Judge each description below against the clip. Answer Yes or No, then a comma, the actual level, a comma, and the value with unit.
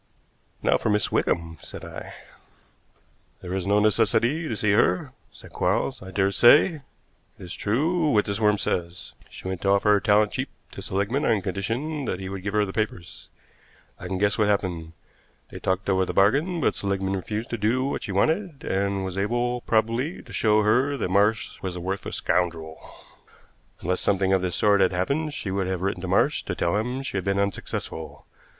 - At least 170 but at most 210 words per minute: Yes, average, 195 wpm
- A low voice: Yes, low, 100 Hz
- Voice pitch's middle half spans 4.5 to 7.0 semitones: No, average, 3.3 semitones